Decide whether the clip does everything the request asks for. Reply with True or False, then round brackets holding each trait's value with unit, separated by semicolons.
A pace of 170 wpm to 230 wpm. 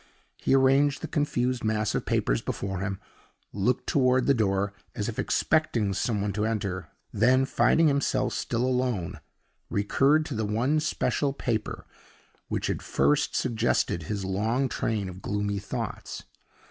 False (145 wpm)